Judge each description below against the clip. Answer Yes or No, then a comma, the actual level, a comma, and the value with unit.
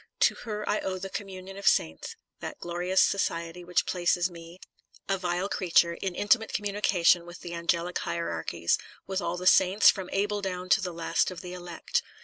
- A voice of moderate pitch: Yes, medium, 180 Hz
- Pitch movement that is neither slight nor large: No, narrow, 2.2 semitones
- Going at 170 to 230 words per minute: Yes, average, 180 wpm